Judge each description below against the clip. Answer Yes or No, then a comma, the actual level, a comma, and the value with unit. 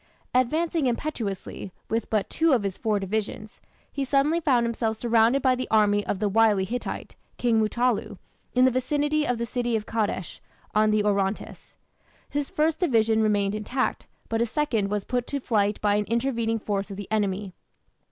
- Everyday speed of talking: Yes, average, 175 wpm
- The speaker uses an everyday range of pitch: Yes, average, 3.6 semitones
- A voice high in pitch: Yes, high, 225 Hz